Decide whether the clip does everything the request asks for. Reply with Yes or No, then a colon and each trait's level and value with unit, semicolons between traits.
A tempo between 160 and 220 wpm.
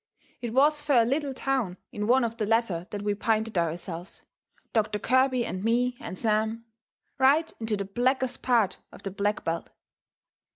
Yes: average, 170 wpm